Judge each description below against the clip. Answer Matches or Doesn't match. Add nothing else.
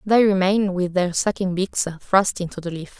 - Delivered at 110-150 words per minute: Doesn't match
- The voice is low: Doesn't match